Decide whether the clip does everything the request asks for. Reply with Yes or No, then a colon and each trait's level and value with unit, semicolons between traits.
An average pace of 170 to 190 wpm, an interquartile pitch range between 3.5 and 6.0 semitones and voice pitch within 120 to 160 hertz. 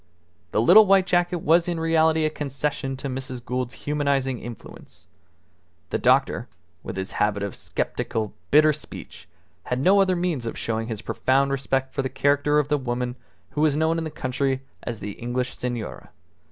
Yes: average, 175 wpm; average, 4.1 semitones; low, 135 Hz